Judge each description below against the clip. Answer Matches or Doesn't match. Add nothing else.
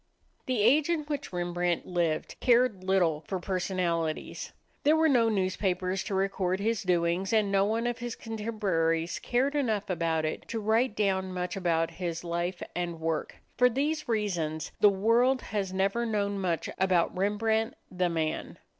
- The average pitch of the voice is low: Doesn't match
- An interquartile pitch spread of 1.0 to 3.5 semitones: Doesn't match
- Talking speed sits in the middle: Matches